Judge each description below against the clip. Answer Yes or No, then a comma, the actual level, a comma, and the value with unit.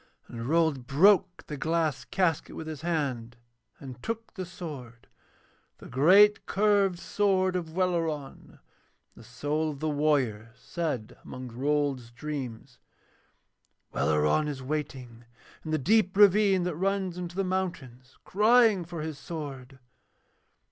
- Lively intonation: Yes, wide, 5.8 semitones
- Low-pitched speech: No, medium, 155 Hz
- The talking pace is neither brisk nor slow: No, slow, 130 wpm